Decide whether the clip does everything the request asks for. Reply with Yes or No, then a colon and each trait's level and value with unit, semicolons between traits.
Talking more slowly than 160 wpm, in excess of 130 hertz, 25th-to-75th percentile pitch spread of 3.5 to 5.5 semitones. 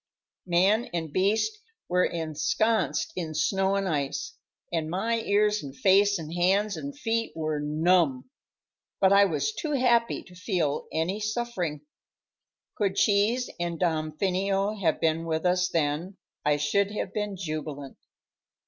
Yes: average, 140 wpm; medium, 185 Hz; average, 4.6 semitones